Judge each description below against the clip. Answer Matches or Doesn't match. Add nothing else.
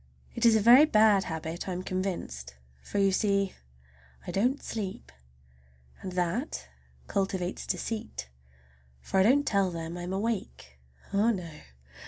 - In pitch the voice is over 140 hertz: Matches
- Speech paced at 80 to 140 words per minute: Matches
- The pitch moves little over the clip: Doesn't match